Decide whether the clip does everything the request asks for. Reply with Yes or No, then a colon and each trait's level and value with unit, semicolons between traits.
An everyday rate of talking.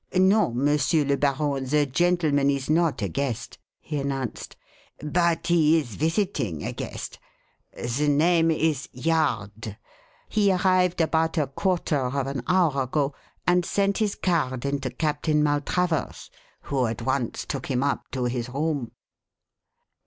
Yes: average, 145 wpm